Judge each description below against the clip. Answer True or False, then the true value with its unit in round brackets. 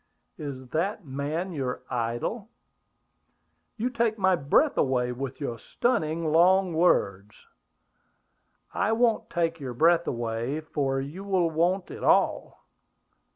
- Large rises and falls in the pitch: True (6.0 semitones)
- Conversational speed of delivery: False (120 wpm)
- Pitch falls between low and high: True (160 Hz)